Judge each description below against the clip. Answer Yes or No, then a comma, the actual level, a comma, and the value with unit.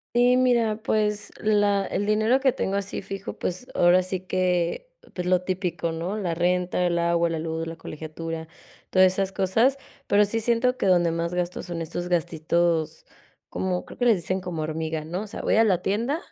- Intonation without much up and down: No, average, 3.6 semitones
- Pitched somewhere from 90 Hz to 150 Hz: No, medium, 185 Hz